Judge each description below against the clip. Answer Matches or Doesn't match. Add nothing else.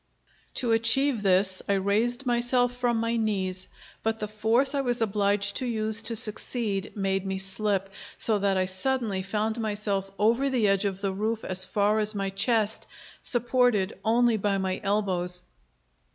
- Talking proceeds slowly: Doesn't match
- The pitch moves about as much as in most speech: Matches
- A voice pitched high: Matches